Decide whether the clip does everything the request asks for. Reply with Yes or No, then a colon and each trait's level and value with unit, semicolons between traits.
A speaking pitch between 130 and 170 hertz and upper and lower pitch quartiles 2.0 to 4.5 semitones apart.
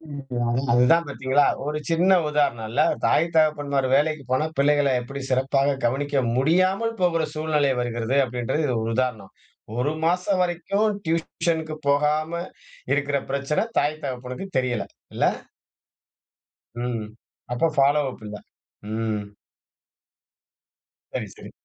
Yes: medium, 140 Hz; average, 3.8 semitones